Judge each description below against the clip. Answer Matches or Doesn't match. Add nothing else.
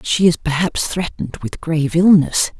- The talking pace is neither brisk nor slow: Matches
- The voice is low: Doesn't match